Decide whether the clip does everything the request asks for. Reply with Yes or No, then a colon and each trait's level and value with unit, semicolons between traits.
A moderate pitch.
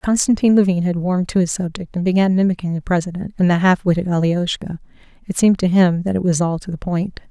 Yes: medium, 180 Hz